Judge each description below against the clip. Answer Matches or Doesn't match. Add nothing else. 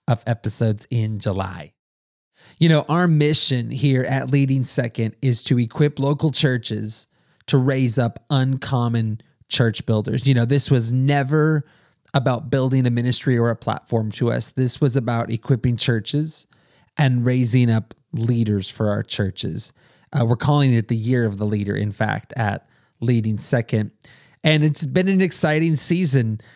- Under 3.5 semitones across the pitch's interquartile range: Doesn't match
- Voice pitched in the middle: Doesn't match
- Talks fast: Doesn't match